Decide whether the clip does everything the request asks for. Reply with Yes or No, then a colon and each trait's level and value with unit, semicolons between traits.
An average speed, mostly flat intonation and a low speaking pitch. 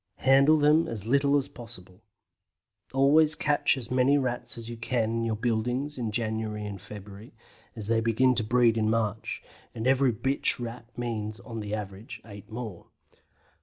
No: average, 165 wpm; average, 3.1 semitones; low, 115 Hz